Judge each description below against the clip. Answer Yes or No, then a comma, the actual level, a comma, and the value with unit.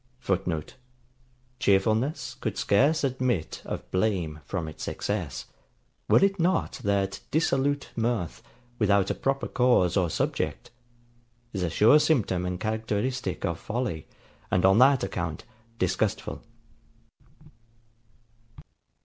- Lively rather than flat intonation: Yes, wide, 6.0 semitones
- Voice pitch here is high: No, low, 105 Hz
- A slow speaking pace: Yes, slow, 110 wpm